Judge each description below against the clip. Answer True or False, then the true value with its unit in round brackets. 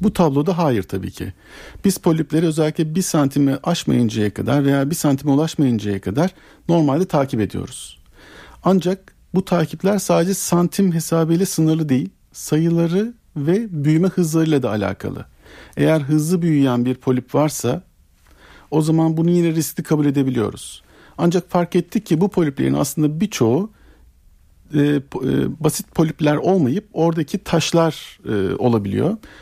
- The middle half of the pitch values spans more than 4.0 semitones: True (5.1 semitones)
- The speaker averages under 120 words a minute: False (125 wpm)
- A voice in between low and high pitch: True (155 Hz)